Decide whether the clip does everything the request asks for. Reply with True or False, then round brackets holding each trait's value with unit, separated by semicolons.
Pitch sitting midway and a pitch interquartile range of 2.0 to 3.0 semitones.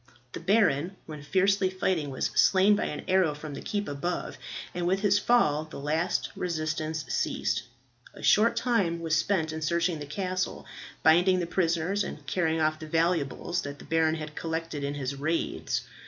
False (165 Hz; 3.4 semitones)